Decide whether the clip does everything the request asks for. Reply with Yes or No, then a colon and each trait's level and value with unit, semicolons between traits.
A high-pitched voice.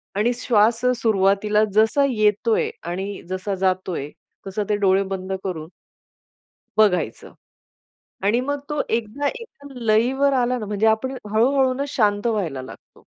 Yes: high, 215 Hz